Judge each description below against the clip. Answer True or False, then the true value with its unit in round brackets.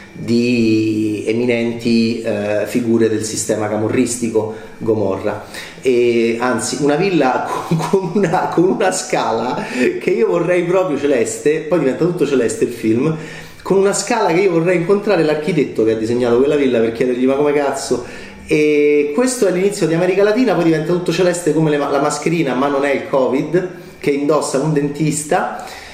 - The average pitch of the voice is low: False (145 Hz)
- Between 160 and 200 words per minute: True (165 wpm)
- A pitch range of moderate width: False (7.2 semitones)